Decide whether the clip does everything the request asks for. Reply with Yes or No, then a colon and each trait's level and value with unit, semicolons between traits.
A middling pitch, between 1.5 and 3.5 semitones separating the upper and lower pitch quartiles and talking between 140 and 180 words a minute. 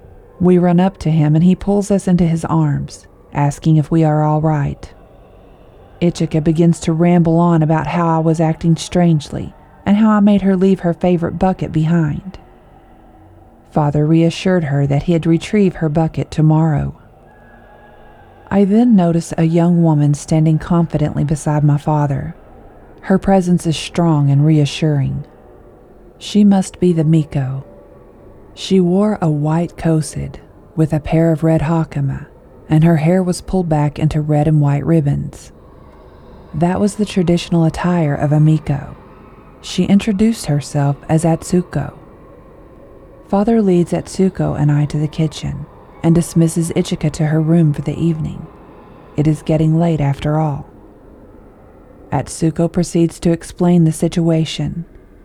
Yes: medium, 160 Hz; average, 2.7 semitones; average, 145 wpm